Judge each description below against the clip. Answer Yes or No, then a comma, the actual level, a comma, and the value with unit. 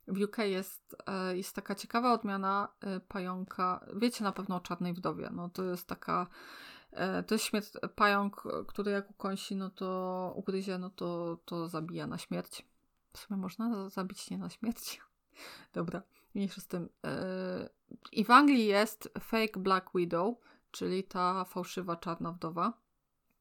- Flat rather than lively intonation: Yes, narrow, 2.0 semitones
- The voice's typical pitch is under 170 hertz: No, high, 195 Hz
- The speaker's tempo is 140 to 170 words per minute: Yes, average, 150 wpm